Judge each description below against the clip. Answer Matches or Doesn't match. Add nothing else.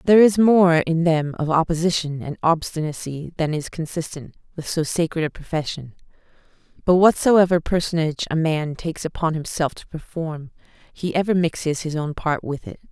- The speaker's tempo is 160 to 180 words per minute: Matches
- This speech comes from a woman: Matches